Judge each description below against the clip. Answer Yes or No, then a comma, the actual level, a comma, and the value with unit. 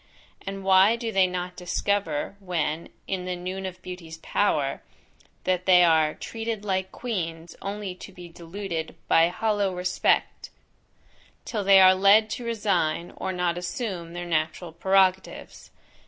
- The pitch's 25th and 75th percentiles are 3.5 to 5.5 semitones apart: No, narrow, 2.4 semitones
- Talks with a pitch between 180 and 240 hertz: Yes, medium, 185 Hz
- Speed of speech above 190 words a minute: No, average, 140 wpm